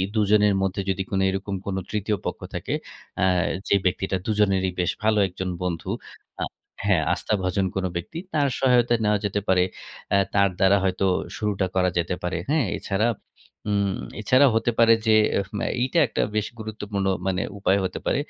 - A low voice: Yes, low, 100 Hz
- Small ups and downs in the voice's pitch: Yes, narrow, 2.2 semitones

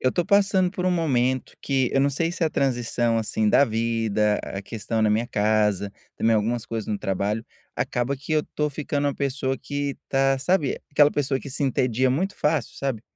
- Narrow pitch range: No, average, 4.3 semitones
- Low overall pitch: Yes, low, 130 Hz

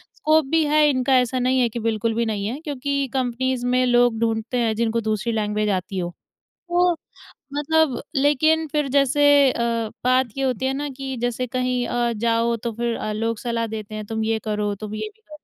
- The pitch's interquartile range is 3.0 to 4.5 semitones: Yes, average, 3.3 semitones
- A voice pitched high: Yes, high, 245 Hz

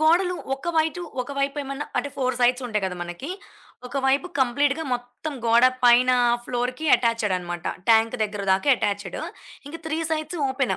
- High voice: Yes, very high, 255 Hz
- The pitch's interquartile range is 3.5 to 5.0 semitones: Yes, average, 4.2 semitones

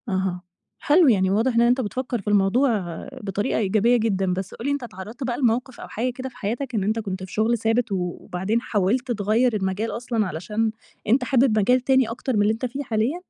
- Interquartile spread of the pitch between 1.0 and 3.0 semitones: No, average, 3.8 semitones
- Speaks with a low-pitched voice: No, high, 225 Hz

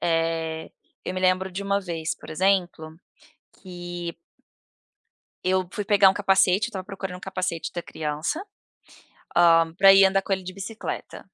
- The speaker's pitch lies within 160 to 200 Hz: Yes, medium, 185 Hz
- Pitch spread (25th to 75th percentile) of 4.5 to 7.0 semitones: No, narrow, 2.4 semitones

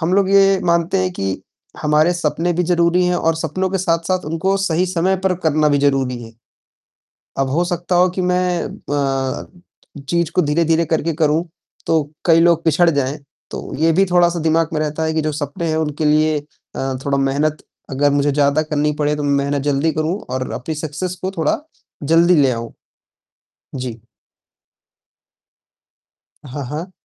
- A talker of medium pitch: Yes, medium, 160 Hz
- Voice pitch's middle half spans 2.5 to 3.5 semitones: Yes, average, 3.0 semitones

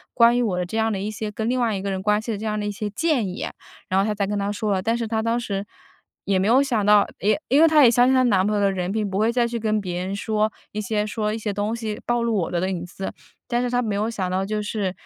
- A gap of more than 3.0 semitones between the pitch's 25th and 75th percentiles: No, average, 2.7 semitones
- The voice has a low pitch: No, high, 210 Hz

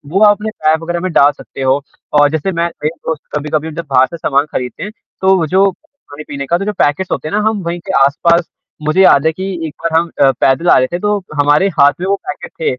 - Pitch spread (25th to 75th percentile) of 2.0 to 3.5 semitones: No, average, 4.7 semitones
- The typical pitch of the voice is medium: Yes, medium, 165 Hz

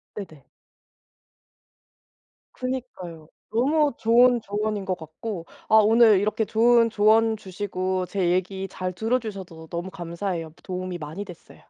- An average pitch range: Yes, average, 3.9 semitones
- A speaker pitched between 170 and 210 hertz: Yes, high, 200 Hz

